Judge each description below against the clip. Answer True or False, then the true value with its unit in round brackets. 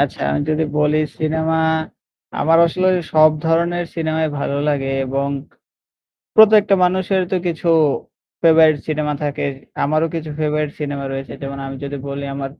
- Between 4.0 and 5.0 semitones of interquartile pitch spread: False (2.5 semitones)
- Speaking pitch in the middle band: True (155 Hz)